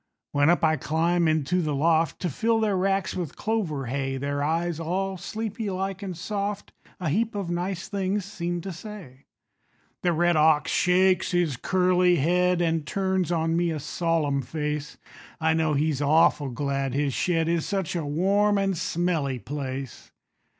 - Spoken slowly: No, average, 165 wpm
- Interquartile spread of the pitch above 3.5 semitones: Yes, average, 3.9 semitones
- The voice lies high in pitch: No, medium, 170 Hz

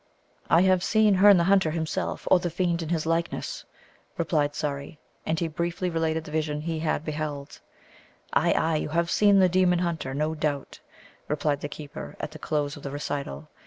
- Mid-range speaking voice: Yes, medium, 160 Hz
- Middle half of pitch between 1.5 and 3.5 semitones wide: Yes, average, 2.7 semitones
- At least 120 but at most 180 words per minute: No, average, 190 wpm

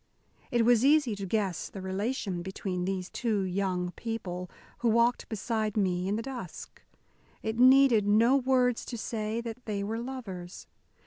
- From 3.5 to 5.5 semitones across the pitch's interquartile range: Yes, average, 3.9 semitones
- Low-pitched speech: No, high, 215 Hz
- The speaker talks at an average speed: Yes, average, 155 wpm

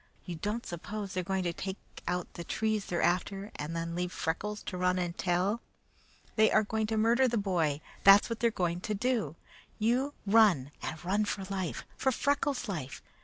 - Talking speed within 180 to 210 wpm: Yes, average, 200 wpm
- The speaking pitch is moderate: No, high, 195 Hz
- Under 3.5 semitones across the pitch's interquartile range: No, average, 3.8 semitones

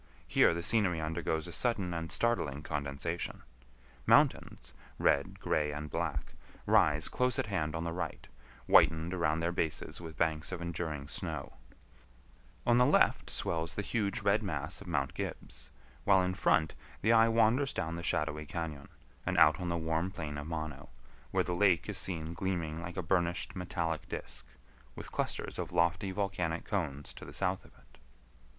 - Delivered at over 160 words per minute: Yes, average, 170 wpm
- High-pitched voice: No, very low, 85 Hz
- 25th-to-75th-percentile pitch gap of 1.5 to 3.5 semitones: Yes, average, 3.2 semitones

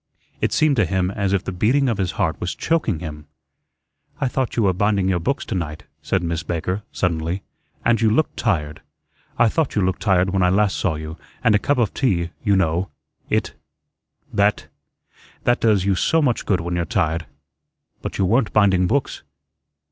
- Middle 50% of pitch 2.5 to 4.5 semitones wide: Yes, average, 4.1 semitones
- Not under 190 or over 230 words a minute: Yes, average, 195 wpm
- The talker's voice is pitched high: No, very low, 95 Hz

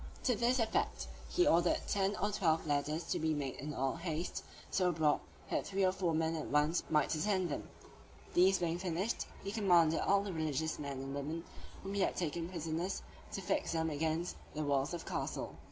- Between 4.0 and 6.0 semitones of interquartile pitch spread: No, average, 3.6 semitones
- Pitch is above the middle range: No, medium, 165 Hz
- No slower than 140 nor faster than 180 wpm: No, average, 200 wpm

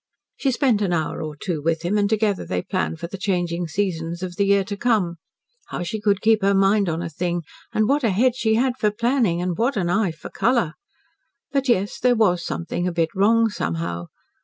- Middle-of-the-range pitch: No, high, 195 Hz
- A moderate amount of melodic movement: Yes, average, 4.4 semitones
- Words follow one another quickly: Yes, fast, 220 wpm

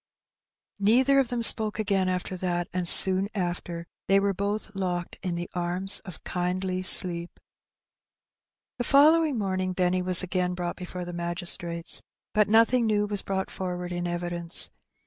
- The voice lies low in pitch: No, medium, 185 Hz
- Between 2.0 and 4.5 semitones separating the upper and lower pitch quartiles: Yes, narrow, 2.5 semitones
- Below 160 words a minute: Yes, average, 150 wpm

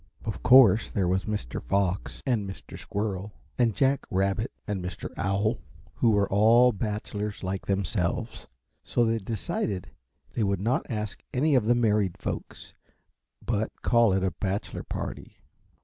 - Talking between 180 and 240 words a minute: No, average, 150 wpm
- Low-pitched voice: Yes, low, 105 Hz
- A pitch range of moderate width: Yes, average, 3.0 semitones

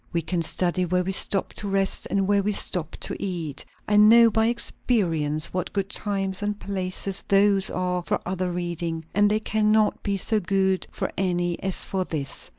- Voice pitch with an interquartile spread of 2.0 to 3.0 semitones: Yes, narrow, 2.5 semitones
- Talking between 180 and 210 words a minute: Yes, average, 185 wpm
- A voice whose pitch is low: No, high, 190 Hz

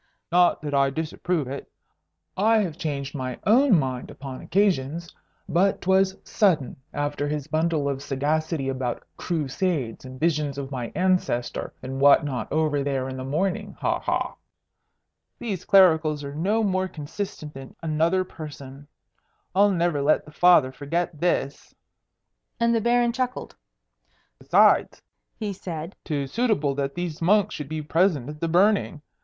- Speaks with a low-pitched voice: No, medium, 155 Hz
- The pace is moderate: Yes, average, 150 wpm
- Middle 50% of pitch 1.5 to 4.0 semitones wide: No, average, 4.9 semitones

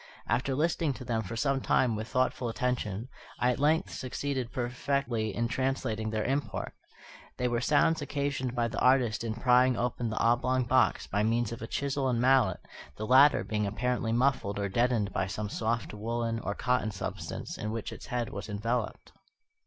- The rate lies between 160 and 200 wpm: Yes, average, 180 wpm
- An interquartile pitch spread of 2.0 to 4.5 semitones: Yes, average, 2.9 semitones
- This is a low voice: Yes, low, 120 Hz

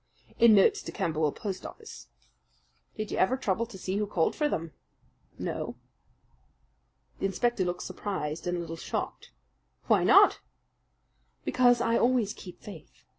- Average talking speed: Yes, average, 145 wpm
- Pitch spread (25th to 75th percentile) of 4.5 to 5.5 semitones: Yes, average, 4.8 semitones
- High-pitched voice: Yes, high, 195 Hz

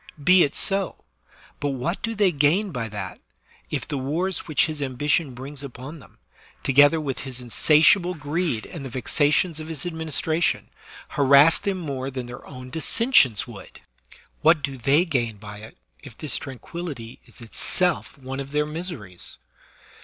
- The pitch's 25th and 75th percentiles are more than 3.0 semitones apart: Yes, average, 4.2 semitones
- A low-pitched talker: No, medium, 145 Hz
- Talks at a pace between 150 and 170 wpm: Yes, average, 165 wpm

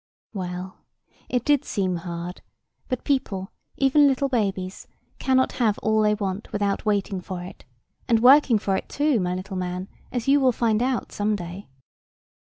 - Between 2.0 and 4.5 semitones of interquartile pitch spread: No, wide, 5.4 semitones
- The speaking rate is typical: Yes, average, 165 wpm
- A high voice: Yes, high, 210 Hz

